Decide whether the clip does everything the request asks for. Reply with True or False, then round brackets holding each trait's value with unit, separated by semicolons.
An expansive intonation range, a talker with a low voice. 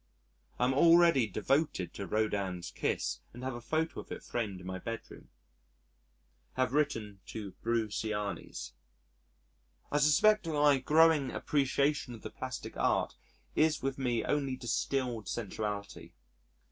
True (5.7 semitones; 125 Hz)